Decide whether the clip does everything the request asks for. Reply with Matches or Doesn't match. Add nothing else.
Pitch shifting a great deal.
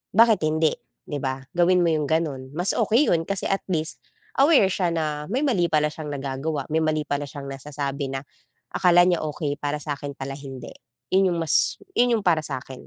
Doesn't match